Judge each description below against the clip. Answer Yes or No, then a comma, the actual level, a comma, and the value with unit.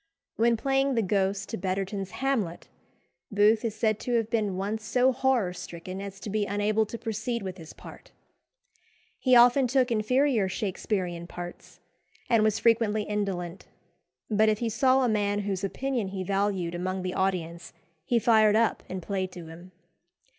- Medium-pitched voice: No, high, 210 Hz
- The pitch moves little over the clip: No, average, 3.4 semitones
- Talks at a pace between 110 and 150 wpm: No, average, 165 wpm